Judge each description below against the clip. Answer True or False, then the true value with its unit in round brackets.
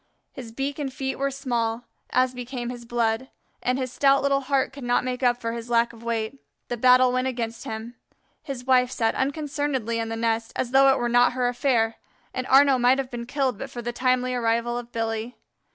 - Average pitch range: False (2.2 semitones)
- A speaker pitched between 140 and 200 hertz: False (245 Hz)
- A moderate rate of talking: False (215 wpm)